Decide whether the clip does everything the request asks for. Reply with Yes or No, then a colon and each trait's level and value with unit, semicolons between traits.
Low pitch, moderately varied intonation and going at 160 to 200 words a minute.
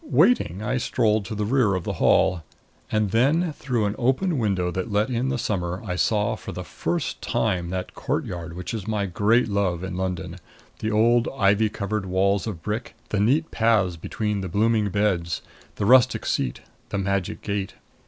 Yes: low, 105 Hz; average, 3.7 semitones; average, 185 wpm